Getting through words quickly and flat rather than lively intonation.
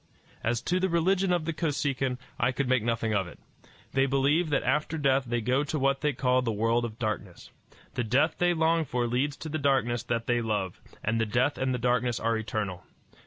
No: fast, 215 wpm; average, 4.1 semitones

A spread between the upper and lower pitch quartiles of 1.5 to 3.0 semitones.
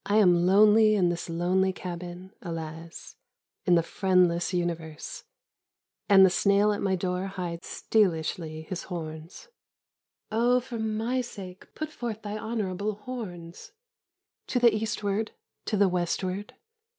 No: average, 3.7 semitones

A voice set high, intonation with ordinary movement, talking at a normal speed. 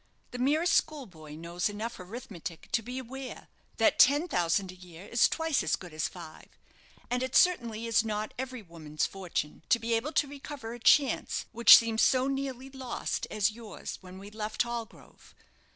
No: high, 230 Hz; wide, 5.7 semitones; average, 175 wpm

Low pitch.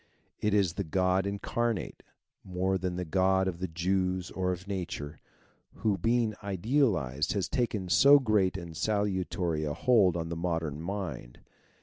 Yes: very low, 95 Hz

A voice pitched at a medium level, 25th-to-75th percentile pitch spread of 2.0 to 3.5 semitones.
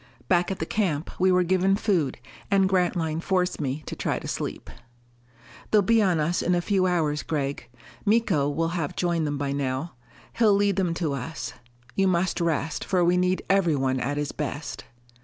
No: medium, 175 Hz; average, 4.1 semitones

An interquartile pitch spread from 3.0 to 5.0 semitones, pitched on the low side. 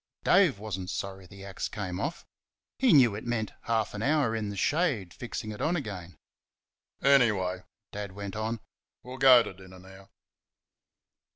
Yes: average, 4.5 semitones; low, 105 Hz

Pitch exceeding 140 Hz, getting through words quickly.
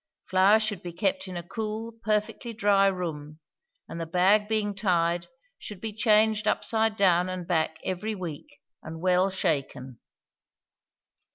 No: high, 190 Hz; average, 145 wpm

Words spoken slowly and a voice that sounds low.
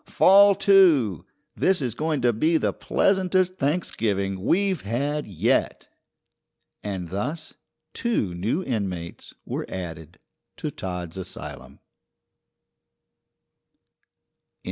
Yes: slow, 95 wpm; low, 125 Hz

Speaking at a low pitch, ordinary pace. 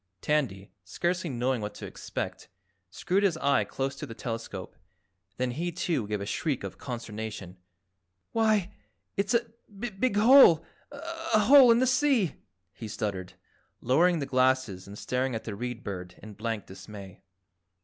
Yes: low, 130 Hz; average, 150 wpm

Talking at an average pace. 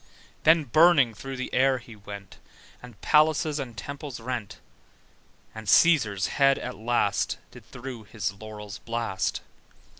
No: slow, 130 wpm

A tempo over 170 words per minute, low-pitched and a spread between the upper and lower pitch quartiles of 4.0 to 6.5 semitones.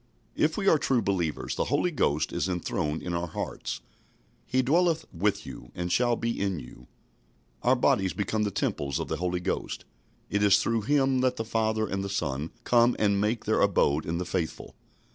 Yes: average, 195 wpm; low, 100 Hz; average, 5.2 semitones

